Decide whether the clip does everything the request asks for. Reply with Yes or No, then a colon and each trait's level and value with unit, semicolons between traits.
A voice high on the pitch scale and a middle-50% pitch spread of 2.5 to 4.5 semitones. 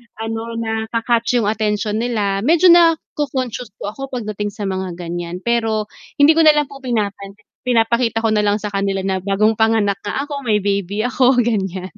Yes: high, 220 Hz; average, 3.4 semitones